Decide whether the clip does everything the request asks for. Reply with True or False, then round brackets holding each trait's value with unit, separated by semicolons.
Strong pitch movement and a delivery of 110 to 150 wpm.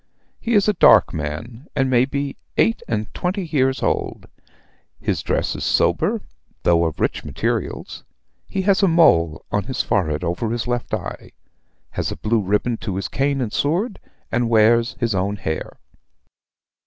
False (6.4 semitones; 165 wpm)